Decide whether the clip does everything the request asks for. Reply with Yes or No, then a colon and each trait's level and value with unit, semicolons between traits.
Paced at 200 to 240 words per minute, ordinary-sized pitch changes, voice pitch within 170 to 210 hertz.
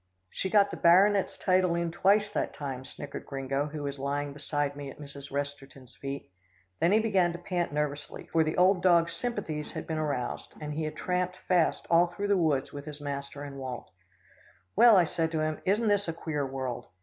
No: fast, 205 wpm; average, 4.3 semitones; medium, 155 Hz